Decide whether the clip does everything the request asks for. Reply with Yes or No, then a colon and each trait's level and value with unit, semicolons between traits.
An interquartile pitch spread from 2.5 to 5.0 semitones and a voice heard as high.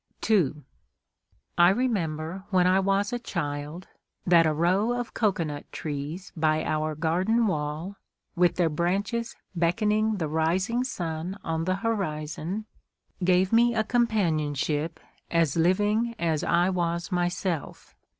No: average, 4.3 semitones; medium, 175 Hz